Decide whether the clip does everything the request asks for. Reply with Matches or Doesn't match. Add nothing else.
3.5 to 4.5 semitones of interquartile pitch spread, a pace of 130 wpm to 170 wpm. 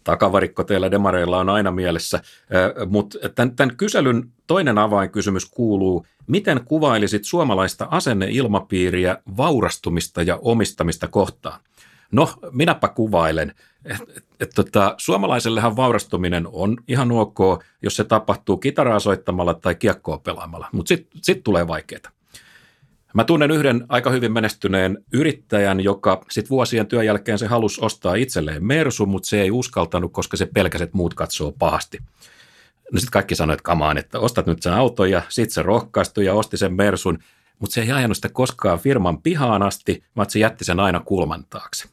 Matches